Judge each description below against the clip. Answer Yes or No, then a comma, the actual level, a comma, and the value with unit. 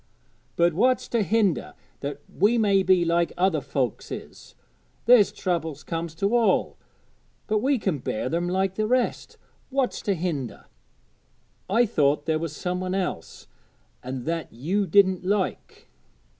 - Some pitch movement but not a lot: Yes, average, 4.5 semitones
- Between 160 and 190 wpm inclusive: No, average, 145 wpm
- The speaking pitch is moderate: Yes, medium, 180 Hz